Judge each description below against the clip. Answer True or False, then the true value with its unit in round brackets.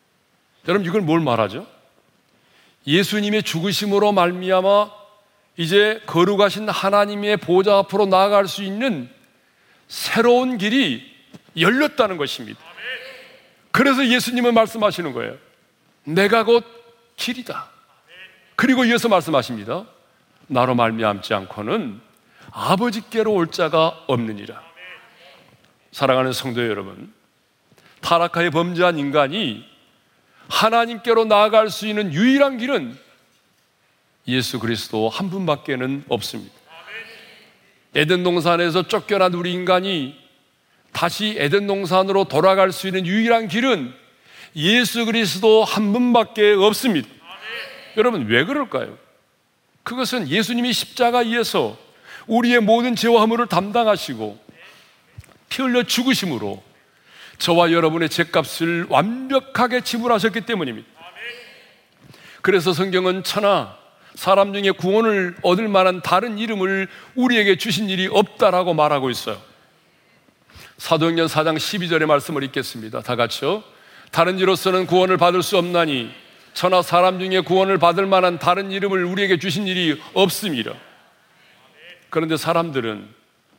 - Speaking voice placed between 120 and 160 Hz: False (190 Hz)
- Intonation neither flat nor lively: True (4.8 semitones)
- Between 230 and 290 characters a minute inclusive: True (275 characters per minute)